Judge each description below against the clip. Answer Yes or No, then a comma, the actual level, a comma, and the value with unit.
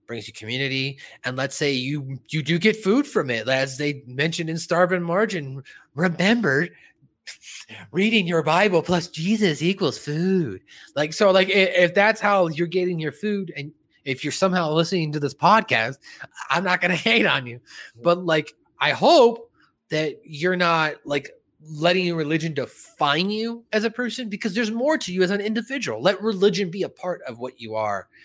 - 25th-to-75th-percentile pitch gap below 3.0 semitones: No, wide, 5.5 semitones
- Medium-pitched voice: Yes, medium, 175 Hz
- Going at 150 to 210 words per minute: Yes, average, 180 wpm